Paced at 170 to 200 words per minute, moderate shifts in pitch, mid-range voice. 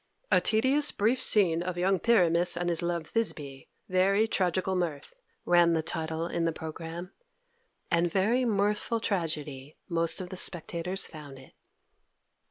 No: average, 145 wpm; average, 3.3 semitones; medium, 175 Hz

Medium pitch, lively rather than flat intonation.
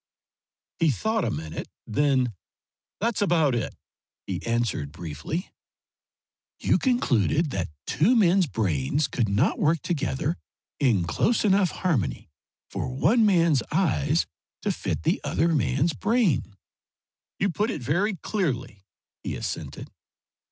Yes: medium, 150 Hz; wide, 8.1 semitones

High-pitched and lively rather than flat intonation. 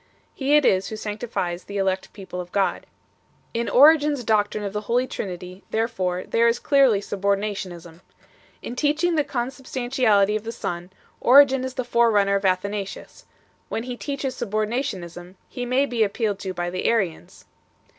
No: high, 215 Hz; average, 4.5 semitones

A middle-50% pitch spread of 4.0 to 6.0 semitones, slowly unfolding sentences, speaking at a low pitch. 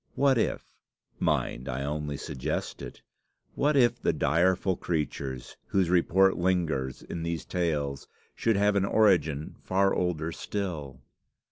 Yes: average, 4.9 semitones; slow, 130 wpm; very low, 85 Hz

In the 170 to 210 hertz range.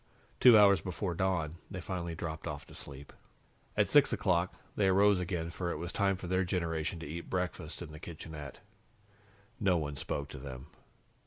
No: very low, 85 Hz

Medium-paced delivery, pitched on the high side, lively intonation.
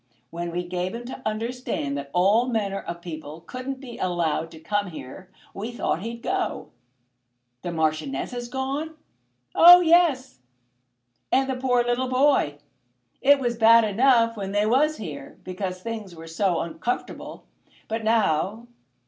Yes: average, 150 wpm; high, 220 Hz; wide, 6.5 semitones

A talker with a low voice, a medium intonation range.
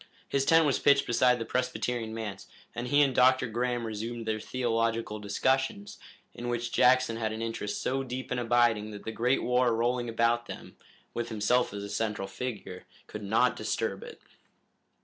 No: low, 120 Hz; narrow, 2.2 semitones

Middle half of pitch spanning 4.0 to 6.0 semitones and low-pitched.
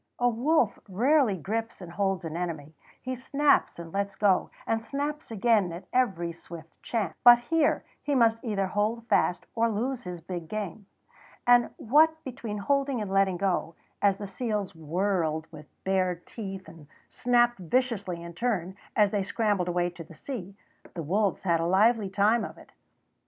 No: average, 5.1 semitones; high, 200 Hz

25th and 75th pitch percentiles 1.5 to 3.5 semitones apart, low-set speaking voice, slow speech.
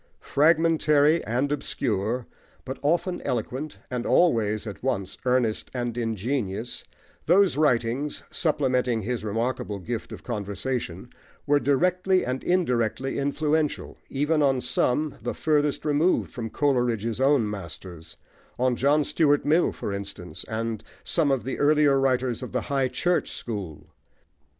No: average, 4.6 semitones; low, 130 Hz; slow, 130 wpm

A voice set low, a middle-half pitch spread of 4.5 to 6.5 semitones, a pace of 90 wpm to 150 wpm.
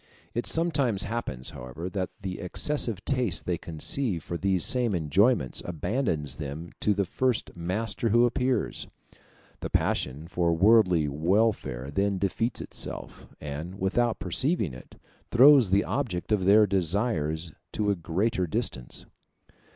Yes: very low, 95 Hz; wide, 5.6 semitones; slow, 135 wpm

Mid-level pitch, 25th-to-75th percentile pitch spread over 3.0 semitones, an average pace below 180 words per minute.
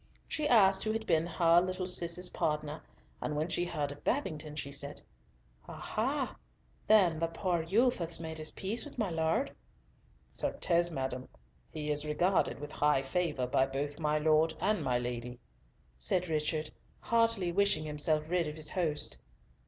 Yes: medium, 160 Hz; average, 3.4 semitones; average, 165 wpm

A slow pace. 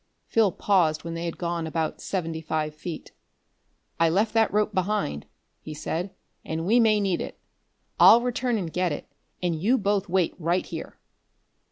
No: average, 170 wpm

